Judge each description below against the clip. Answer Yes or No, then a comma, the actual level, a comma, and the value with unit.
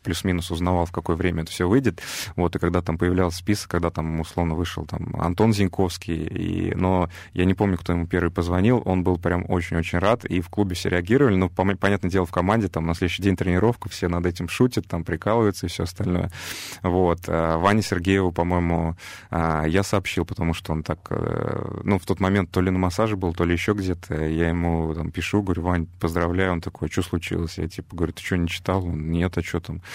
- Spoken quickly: Yes, fast, 215 wpm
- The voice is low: Yes, very low, 90 Hz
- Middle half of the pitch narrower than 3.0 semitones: Yes, narrow, 2.4 semitones